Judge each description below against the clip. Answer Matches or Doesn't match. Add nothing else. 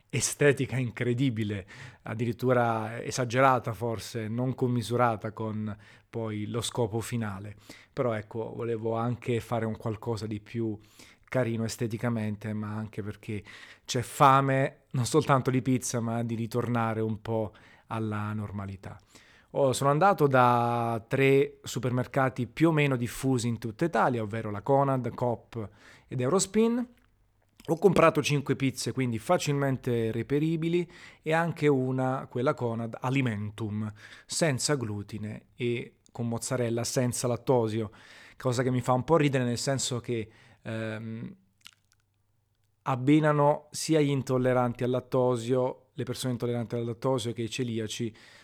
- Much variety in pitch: Doesn't match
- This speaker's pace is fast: Doesn't match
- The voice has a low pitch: Matches